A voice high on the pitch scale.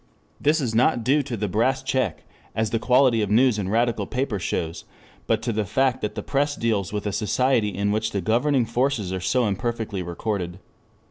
No: low, 110 Hz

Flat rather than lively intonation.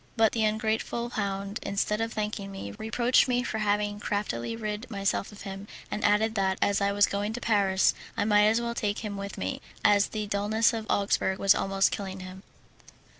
Yes: narrow, 1.7 semitones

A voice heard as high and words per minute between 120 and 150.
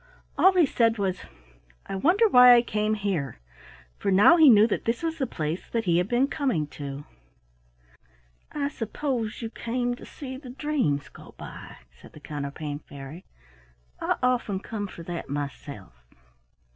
No: high, 215 Hz; average, 160 wpm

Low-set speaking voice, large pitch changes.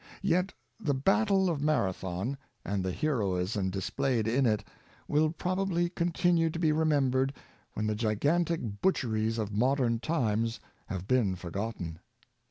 Yes: low, 130 Hz; wide, 7.6 semitones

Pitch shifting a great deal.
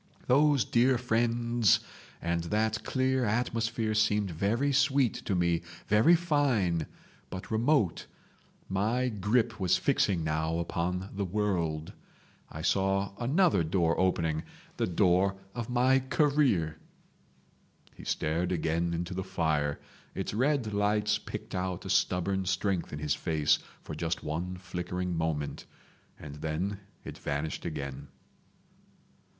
Yes: wide, 5.8 semitones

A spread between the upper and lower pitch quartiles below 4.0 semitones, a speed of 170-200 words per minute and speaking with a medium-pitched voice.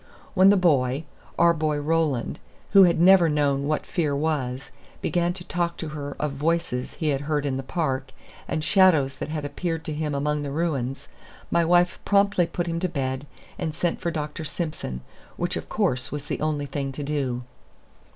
Yes: average, 3.3 semitones; average, 190 wpm; medium, 150 Hz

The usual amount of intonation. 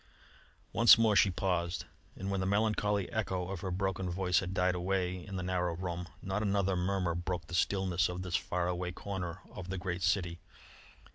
No: narrow, 1.5 semitones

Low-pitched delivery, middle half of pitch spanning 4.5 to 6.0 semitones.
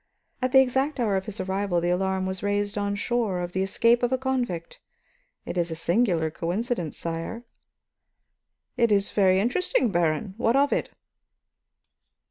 No: high, 200 Hz; average, 5.1 semitones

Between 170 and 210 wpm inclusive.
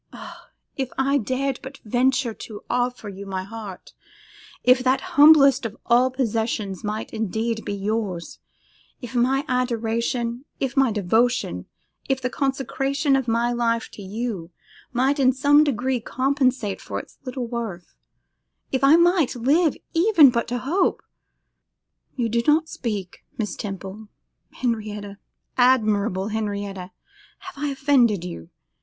No: slow, 135 wpm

